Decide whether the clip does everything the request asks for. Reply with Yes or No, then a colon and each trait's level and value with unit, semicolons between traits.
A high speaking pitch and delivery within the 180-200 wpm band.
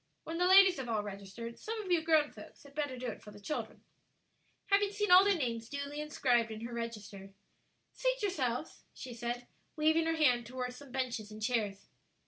Yes: very high, 255 Hz; average, 195 wpm